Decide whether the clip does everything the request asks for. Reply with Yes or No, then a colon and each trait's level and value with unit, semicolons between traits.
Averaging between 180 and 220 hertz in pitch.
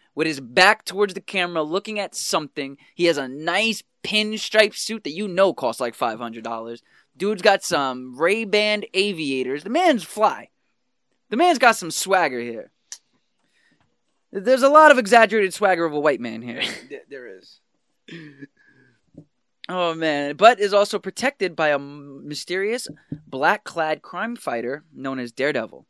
Yes: high, 190 Hz